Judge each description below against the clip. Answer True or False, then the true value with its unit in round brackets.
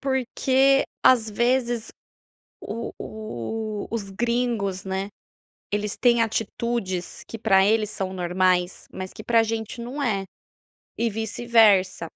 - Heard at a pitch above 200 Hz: True (220 Hz)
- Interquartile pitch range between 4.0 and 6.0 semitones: False (3.5 semitones)